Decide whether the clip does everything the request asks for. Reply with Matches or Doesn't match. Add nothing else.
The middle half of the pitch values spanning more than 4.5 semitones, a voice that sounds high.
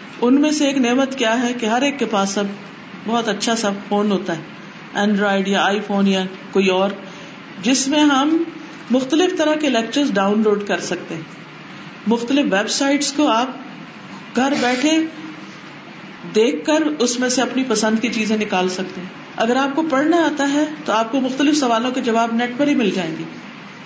Matches